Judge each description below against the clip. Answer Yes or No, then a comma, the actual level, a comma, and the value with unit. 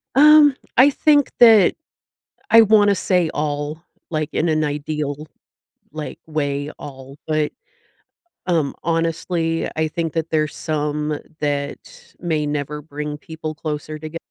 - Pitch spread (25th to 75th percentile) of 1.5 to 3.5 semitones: Yes, narrow, 2.4 semitones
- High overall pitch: No, medium, 155 Hz